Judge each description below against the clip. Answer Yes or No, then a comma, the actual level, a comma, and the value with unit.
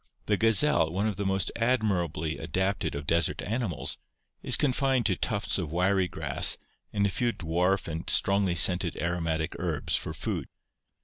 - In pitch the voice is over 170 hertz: No, very low, 95 Hz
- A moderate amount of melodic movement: Yes, average, 3.9 semitones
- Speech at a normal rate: Yes, average, 160 wpm